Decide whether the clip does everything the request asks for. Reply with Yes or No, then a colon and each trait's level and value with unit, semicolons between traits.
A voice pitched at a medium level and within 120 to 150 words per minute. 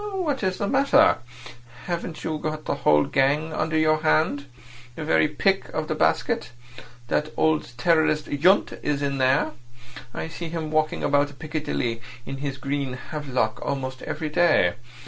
Yes: medium, 155 Hz; average, 145 wpm